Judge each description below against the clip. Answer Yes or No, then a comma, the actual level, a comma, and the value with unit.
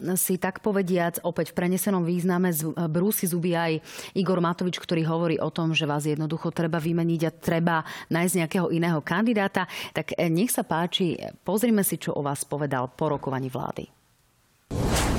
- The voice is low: No, medium, 170 Hz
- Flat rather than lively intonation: Yes, narrow, 2.3 semitones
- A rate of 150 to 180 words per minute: Yes, average, 160 wpm